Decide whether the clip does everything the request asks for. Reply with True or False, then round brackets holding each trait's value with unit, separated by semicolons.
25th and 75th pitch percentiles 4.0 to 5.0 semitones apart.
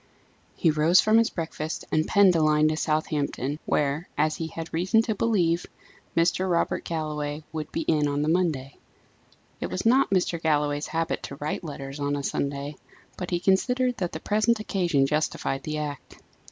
False (3.5 semitones)